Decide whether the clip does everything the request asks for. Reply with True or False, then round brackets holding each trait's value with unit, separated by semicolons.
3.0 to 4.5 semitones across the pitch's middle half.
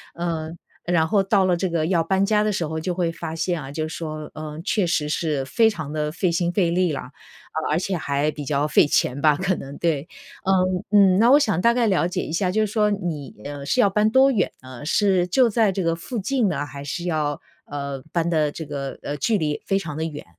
True (4.2 semitones)